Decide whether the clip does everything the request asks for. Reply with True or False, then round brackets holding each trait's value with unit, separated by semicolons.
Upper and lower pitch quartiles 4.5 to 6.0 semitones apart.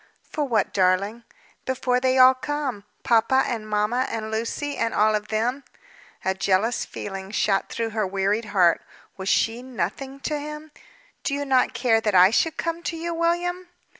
True (4.9 semitones)